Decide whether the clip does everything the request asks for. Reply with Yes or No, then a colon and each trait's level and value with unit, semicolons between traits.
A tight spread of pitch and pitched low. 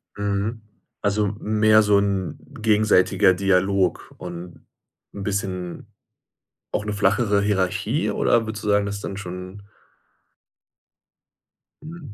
Yes: narrow, 1.8 semitones; low, 100 Hz